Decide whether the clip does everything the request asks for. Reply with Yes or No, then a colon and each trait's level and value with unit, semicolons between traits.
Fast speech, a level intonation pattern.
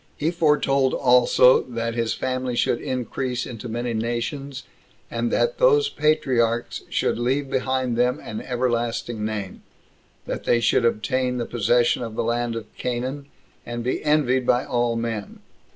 No: average, 150 wpm; narrow, 1.9 semitones